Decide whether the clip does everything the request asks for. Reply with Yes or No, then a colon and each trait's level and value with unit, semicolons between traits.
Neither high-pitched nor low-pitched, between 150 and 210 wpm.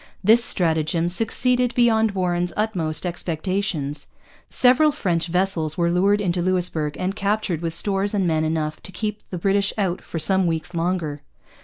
Yes: medium, 180 Hz; average, 160 wpm